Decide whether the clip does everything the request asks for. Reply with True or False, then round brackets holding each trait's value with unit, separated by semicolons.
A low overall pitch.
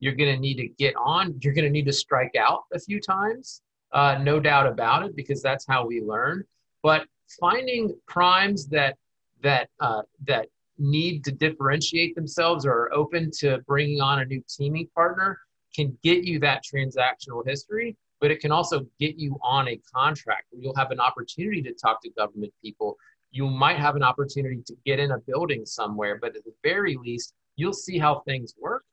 False (145 Hz)